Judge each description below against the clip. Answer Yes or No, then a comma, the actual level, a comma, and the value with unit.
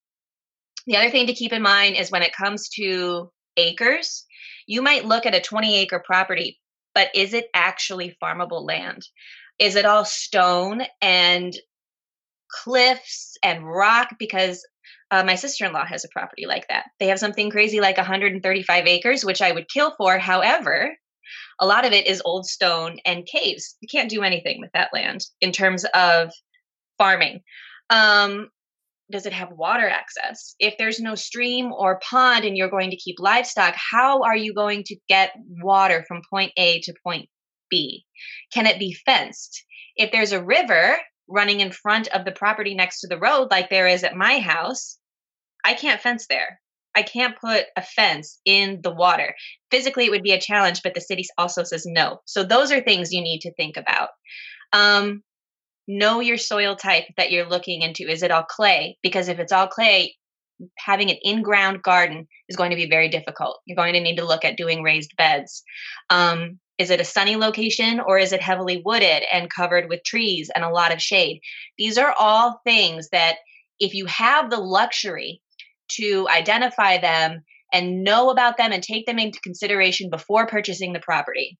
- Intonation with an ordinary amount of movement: Yes, average, 3.5 semitones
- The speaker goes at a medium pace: Yes, average, 185 wpm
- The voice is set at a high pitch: Yes, high, 195 Hz